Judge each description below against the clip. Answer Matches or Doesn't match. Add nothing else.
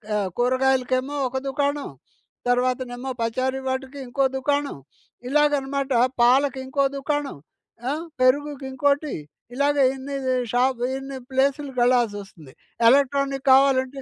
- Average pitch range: Doesn't match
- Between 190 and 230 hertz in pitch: Doesn't match